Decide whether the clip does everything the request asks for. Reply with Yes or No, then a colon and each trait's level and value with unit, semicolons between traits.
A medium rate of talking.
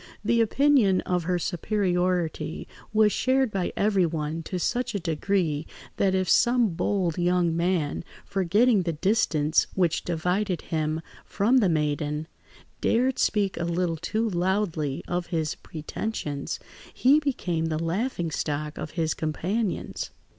No: slow, 130 wpm